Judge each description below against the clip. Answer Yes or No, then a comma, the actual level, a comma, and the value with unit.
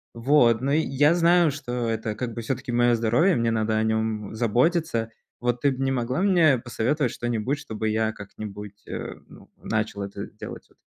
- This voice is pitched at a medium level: No, low, 120 Hz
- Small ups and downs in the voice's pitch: No, average, 3.8 semitones